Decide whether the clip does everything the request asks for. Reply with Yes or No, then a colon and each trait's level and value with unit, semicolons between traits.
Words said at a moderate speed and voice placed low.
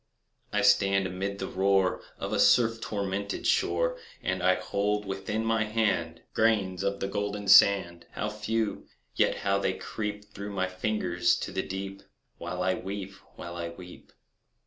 Yes: average, 155 wpm; low, 100 Hz